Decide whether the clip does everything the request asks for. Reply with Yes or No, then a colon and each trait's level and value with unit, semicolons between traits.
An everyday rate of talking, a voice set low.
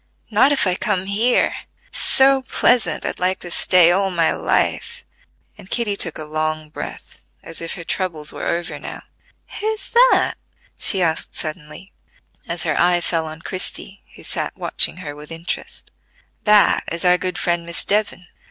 No: average, 170 wpm; medium, 180 Hz